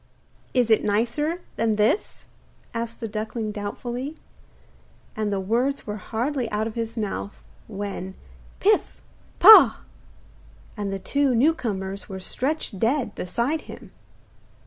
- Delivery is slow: Yes, slow, 125 wpm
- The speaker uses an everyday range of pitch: Yes, average, 3.4 semitones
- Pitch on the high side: Yes, high, 225 Hz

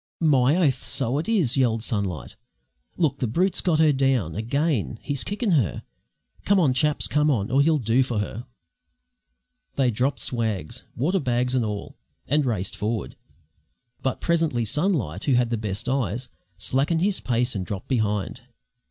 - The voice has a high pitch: No, low, 130 Hz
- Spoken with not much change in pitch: No, average, 5.1 semitones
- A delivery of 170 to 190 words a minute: No, average, 160 wpm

